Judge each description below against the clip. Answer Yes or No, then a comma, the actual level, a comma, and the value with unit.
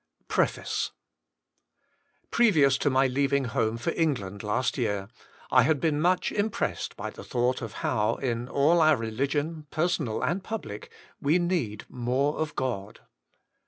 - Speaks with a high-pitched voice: No, low, 135 Hz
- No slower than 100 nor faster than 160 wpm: Yes, average, 150 wpm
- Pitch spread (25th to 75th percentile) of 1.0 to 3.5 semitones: No, average, 5.2 semitones